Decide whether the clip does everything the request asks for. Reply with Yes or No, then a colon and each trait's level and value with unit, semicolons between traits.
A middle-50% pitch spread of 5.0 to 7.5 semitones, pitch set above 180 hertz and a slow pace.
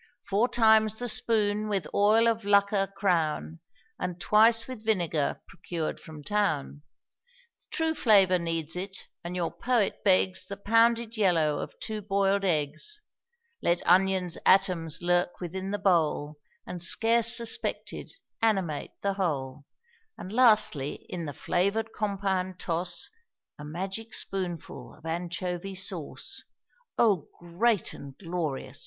No: average, 3.9 semitones; high, 190 Hz; slow, 125 wpm